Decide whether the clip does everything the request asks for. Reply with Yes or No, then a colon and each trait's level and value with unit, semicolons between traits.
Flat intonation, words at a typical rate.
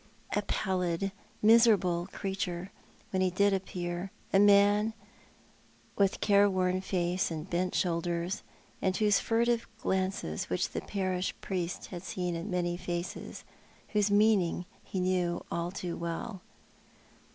No: narrow, 2.3 semitones; slow, 130 wpm